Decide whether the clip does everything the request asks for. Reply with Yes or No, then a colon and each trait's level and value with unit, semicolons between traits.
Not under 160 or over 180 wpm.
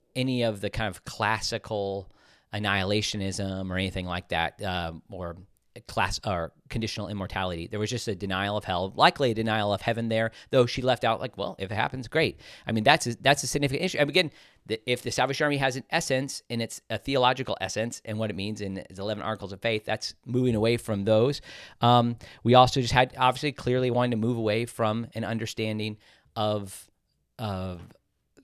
No: average, 195 wpm